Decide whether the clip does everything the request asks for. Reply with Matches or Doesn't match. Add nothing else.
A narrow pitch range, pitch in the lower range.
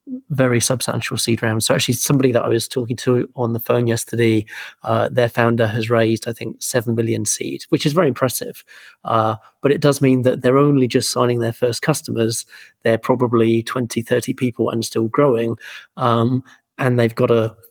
Matches